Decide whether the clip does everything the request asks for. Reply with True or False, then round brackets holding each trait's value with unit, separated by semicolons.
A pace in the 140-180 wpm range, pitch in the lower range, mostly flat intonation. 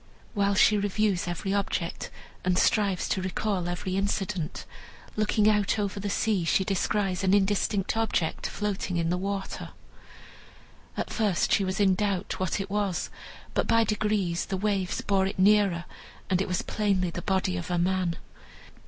False (160 wpm; 195 Hz; 2.1 semitones)